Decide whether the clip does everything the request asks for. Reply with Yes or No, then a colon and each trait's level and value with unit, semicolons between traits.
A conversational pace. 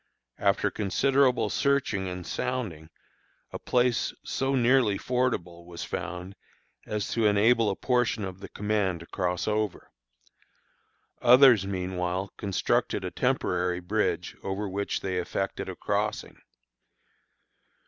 No: slow, 115 wpm